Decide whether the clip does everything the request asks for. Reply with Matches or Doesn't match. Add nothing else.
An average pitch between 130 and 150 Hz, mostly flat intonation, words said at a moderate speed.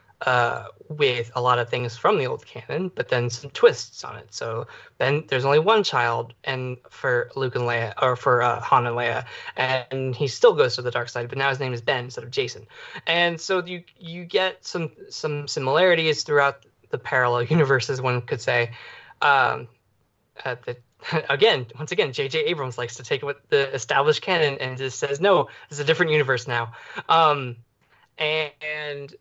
Doesn't match